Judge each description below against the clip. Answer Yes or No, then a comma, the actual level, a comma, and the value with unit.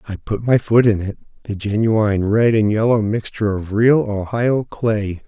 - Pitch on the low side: Yes, low, 110 Hz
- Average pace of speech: Yes, average, 170 wpm